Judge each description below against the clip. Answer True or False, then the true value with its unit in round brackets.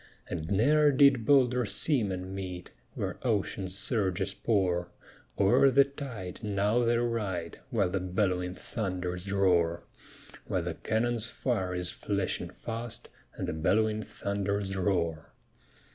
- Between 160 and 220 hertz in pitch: False (100 Hz)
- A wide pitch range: False (4.2 semitones)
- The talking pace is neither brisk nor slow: False (125 wpm)